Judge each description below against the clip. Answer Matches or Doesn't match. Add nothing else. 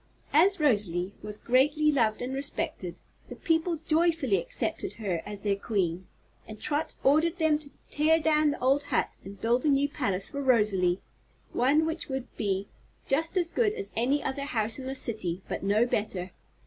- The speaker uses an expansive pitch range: Matches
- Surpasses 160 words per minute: Matches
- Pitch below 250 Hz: Doesn't match